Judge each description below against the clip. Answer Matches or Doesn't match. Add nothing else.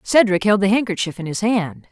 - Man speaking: Doesn't match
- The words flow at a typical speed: Doesn't match